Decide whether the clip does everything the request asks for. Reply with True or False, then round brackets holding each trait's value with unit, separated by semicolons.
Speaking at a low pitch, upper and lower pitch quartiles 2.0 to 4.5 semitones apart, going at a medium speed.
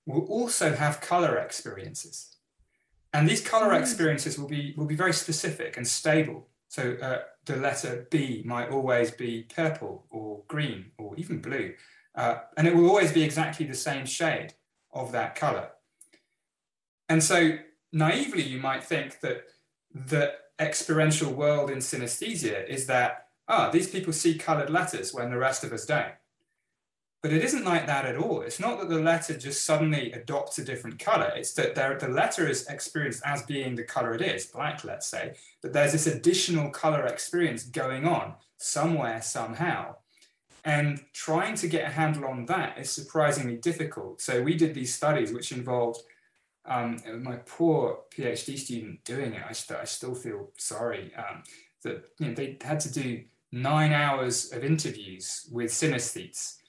False (150 Hz; 3.8 semitones; 170 wpm)